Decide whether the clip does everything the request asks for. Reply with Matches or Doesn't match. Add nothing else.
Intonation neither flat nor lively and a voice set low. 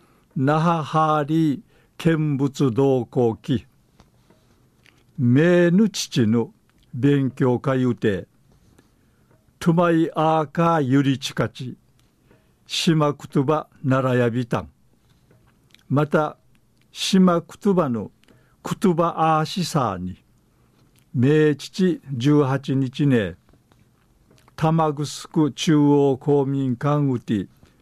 Doesn't match